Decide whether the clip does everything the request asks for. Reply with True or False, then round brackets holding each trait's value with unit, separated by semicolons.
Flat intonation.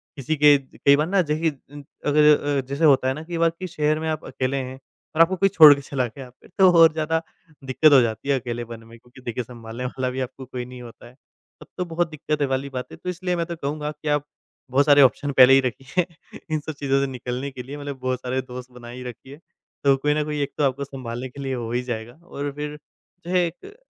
False (3.2 semitones)